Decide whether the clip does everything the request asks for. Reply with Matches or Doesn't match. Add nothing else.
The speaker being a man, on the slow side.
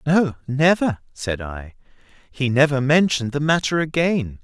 Matches